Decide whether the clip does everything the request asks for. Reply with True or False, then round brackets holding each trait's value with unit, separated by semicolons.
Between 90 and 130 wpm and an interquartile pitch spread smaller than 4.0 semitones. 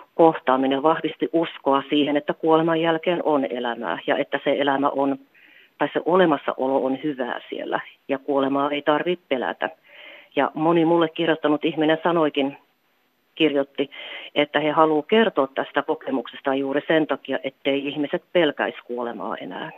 False (140 wpm; 2.7 semitones)